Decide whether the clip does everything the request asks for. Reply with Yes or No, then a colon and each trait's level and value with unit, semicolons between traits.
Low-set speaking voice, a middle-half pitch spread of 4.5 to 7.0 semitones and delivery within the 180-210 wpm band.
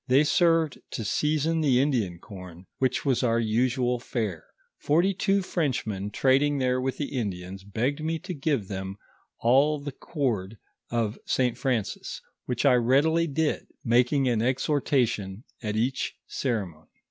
No: low, 125 Hz; average, 4.9 semitones; average, 145 wpm